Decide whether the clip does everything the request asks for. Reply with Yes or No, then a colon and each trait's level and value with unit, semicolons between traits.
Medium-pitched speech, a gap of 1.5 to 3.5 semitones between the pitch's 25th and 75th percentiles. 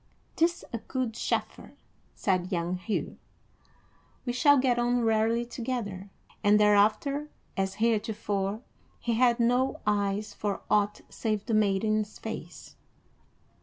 No: high, 215 Hz; average, 3.0 semitones